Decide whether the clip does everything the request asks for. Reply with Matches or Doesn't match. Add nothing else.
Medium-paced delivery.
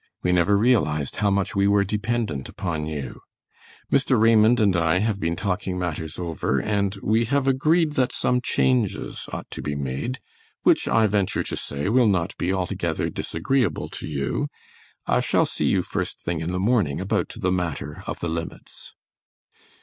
Matches